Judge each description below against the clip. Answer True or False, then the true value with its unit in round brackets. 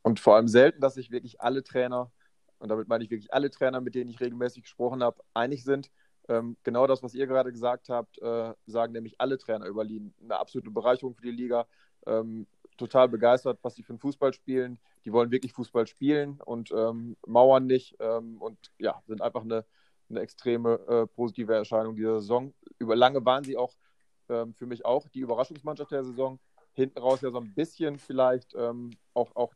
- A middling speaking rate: False (195 wpm)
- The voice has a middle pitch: False (125 Hz)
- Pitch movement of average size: False (2.1 semitones)